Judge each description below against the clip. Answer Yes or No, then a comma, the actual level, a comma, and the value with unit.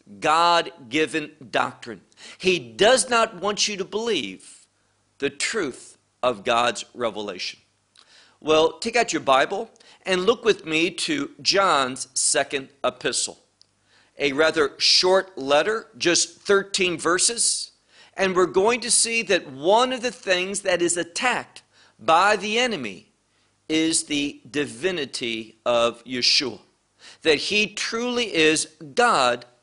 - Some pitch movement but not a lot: No, wide, 7.6 semitones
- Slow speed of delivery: Yes, slow, 125 wpm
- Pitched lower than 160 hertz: No, medium, 170 Hz